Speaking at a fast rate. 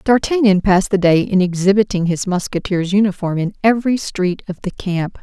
No: average, 170 wpm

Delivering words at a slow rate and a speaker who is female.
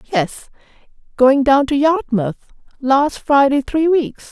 Yes: slow, 125 wpm; female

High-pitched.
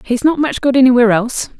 Yes: very high, 250 Hz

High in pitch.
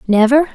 Yes: very high, 255 Hz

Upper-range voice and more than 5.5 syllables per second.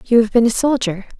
Yes: high, 230 Hz; 6.1 syllables/s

